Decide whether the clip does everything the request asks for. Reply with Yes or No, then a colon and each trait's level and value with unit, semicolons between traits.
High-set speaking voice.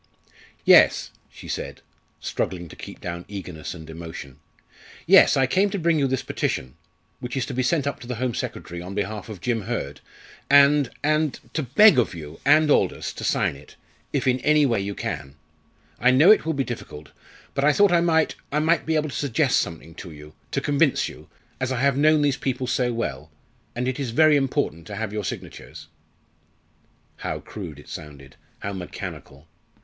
No: low, 125 Hz